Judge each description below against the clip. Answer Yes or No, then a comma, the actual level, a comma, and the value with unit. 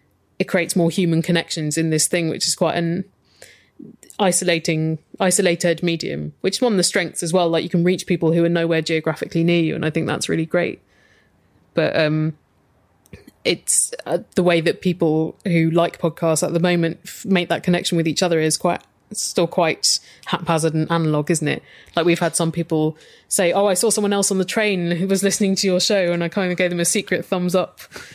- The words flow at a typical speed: No, fast, 215 wpm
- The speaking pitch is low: No, medium, 170 Hz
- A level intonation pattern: Yes, narrow, 2.1 semitones